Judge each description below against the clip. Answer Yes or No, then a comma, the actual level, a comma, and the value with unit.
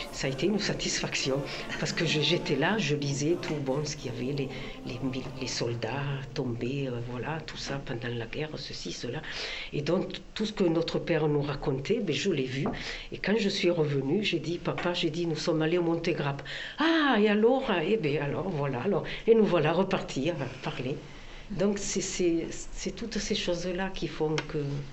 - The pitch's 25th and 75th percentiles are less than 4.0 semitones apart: No, average, 4.5 semitones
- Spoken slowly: No, average, 200 wpm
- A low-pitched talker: No, medium, 160 Hz